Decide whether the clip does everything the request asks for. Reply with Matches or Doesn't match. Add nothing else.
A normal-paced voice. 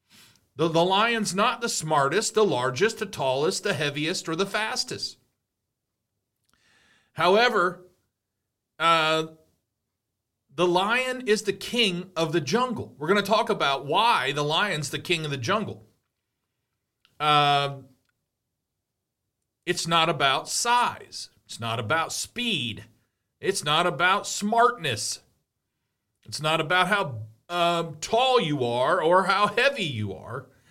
Doesn't match